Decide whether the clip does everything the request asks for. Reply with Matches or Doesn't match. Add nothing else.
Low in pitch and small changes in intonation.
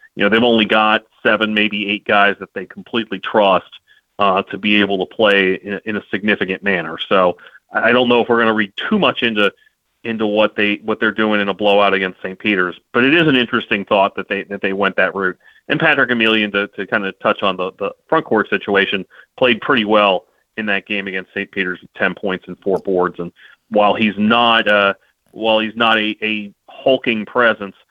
Matches